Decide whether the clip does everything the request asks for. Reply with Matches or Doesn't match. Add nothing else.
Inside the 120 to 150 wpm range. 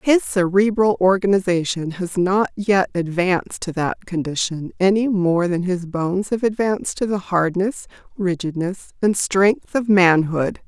Matches